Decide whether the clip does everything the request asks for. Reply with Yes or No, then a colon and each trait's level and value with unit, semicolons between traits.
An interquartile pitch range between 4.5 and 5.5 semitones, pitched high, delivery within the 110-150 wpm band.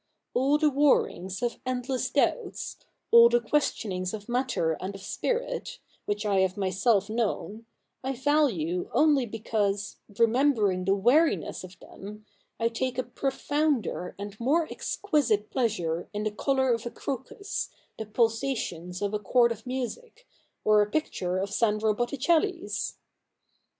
Yes: average, 4.9 semitones; high, 230 Hz; average, 140 wpm